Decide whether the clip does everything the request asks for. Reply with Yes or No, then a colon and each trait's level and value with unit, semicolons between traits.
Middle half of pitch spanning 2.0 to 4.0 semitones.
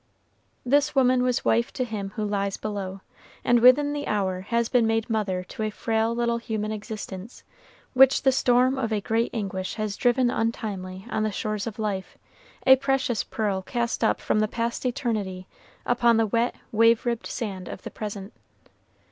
Yes: average, 2.8 semitones